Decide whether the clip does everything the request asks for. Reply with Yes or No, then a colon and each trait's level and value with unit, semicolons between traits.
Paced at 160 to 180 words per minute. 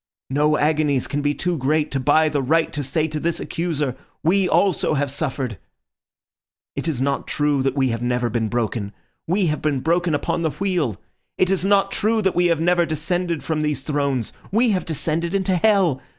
No: average, 195 wpm